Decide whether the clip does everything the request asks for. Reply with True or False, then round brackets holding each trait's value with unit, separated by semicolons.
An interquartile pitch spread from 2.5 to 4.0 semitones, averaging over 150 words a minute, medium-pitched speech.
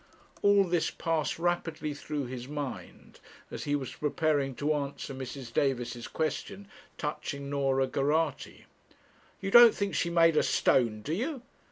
False (3.7 semitones; 145 wpm; 150 Hz)